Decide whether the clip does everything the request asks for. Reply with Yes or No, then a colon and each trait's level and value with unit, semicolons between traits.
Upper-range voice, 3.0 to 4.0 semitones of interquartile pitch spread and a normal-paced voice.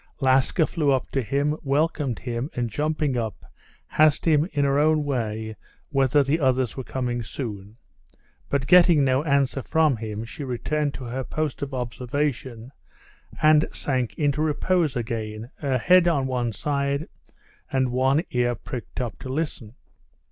No: low, 135 Hz; average, 3.4 semitones; average, 155 wpm